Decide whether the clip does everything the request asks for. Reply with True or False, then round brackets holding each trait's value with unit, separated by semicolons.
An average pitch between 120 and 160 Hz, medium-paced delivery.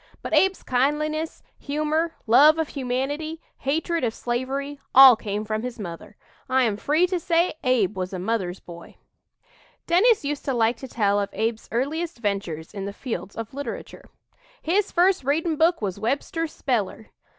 False (265 Hz; 160 wpm)